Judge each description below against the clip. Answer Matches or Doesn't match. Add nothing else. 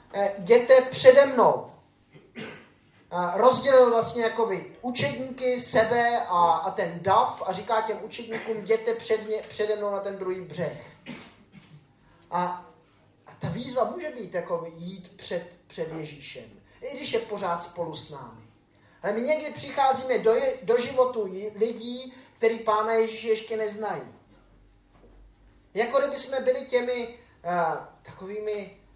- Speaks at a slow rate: Doesn't match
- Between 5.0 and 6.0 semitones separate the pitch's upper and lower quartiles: Matches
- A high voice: Matches